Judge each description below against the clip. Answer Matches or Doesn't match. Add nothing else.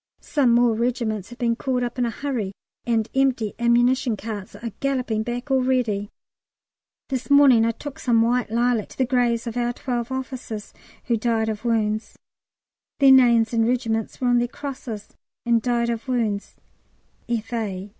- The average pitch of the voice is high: Matches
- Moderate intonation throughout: Doesn't match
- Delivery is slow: Doesn't match